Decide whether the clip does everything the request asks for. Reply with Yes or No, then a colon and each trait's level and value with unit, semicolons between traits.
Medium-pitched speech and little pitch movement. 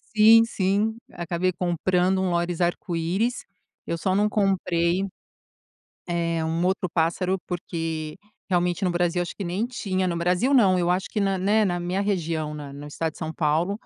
Yes: medium, 180 Hz; narrow, 2.3 semitones